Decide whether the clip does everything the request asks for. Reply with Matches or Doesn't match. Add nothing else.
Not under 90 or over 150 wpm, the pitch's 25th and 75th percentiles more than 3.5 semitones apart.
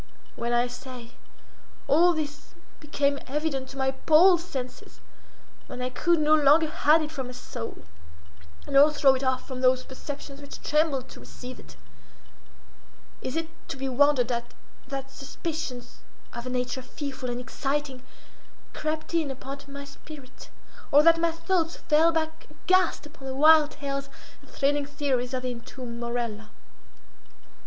Doesn't match